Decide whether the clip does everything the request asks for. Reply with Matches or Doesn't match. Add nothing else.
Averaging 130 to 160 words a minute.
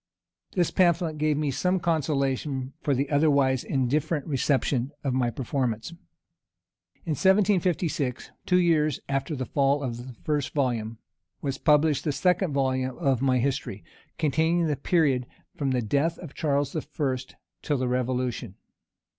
Matches